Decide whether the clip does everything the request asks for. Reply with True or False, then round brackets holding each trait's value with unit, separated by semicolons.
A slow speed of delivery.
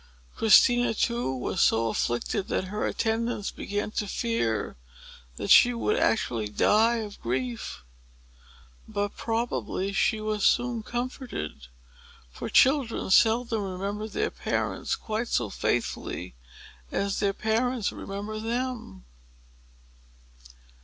True (110 wpm)